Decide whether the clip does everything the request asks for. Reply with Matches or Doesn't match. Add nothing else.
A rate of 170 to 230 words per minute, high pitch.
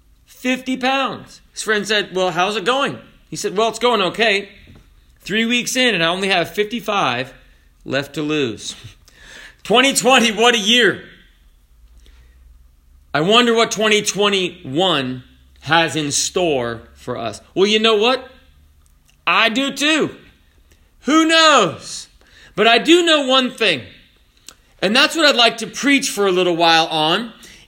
Doesn't match